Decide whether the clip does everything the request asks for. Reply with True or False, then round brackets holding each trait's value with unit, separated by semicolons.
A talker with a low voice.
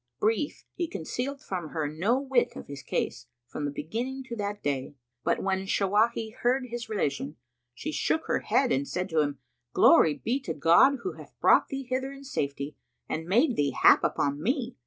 False (210 Hz)